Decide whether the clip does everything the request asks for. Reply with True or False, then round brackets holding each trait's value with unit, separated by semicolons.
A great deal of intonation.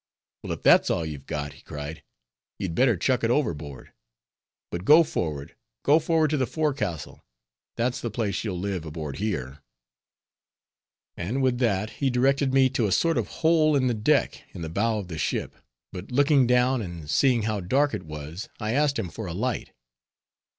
True (7.7 semitones)